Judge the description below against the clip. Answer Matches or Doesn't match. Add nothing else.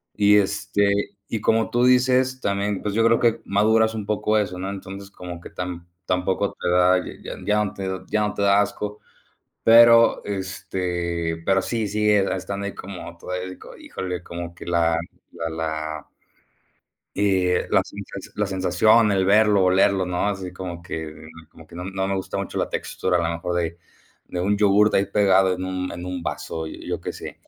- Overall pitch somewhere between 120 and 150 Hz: Doesn't match